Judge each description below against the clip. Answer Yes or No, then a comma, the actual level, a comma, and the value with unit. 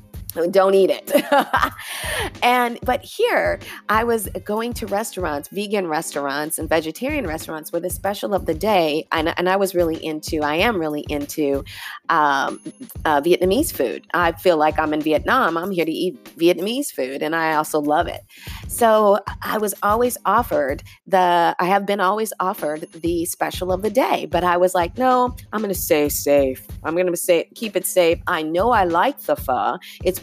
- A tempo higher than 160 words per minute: Yes, average, 180 wpm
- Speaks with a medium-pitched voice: Yes, medium, 180 Hz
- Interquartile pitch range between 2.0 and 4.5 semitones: No, average, 5.2 semitones